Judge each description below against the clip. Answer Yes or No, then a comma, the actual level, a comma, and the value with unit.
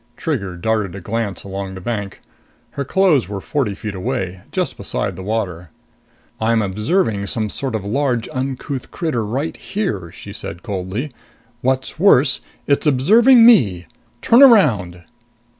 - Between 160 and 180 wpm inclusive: No, average, 140 wpm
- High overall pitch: No, low, 110 Hz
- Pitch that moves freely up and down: Yes, wide, 6.3 semitones